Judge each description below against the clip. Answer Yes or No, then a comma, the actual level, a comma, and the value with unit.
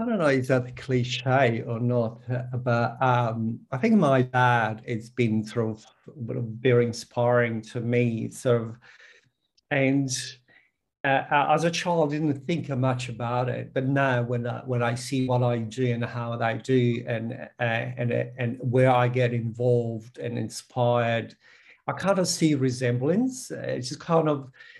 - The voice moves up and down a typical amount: No, narrow, 2.1 semitones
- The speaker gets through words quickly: No, average, 165 wpm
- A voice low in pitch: Yes, low, 125 Hz